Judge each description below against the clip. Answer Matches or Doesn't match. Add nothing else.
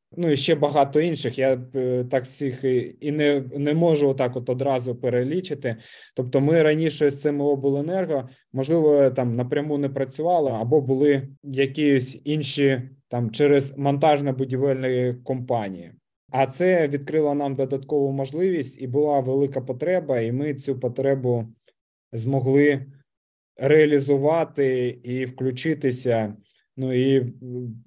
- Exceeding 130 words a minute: Doesn't match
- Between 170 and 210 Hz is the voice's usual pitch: Doesn't match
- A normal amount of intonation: Doesn't match